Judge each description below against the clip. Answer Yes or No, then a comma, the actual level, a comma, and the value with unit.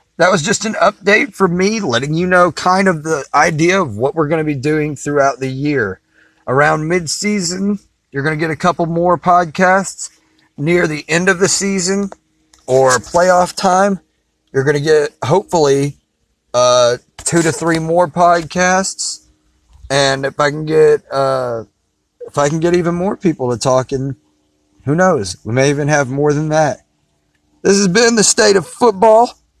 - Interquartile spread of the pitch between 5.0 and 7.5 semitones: Yes, wide, 5.5 semitones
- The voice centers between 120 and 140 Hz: No, medium, 155 Hz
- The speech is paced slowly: No, average, 175 wpm